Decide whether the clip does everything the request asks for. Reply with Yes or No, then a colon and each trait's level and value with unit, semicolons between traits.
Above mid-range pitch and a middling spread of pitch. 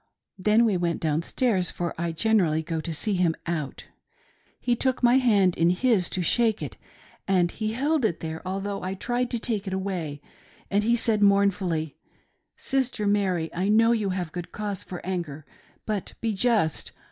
Yes: high, 195 Hz; average, 4.4 semitones